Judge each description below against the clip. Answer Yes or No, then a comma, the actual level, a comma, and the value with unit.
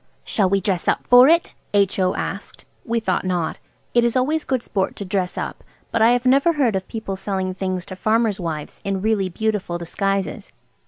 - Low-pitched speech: No, high, 200 Hz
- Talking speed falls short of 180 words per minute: No, average, 195 wpm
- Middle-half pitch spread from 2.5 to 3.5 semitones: No, average, 3.9 semitones